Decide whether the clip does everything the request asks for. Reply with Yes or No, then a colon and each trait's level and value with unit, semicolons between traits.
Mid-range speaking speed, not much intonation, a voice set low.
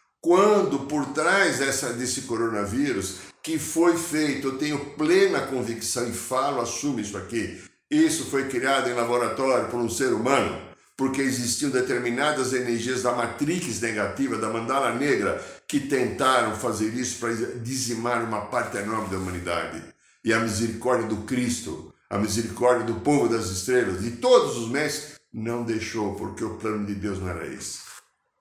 No: average, 155 wpm; average, 3.5 semitones; low, 120 Hz